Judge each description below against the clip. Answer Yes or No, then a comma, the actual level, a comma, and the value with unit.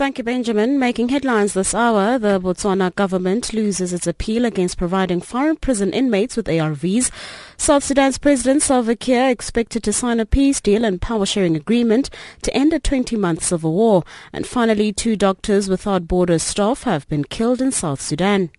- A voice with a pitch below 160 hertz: No, high, 215 Hz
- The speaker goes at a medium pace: Yes, average, 170 wpm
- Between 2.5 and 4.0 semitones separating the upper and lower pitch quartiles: No, average, 4.9 semitones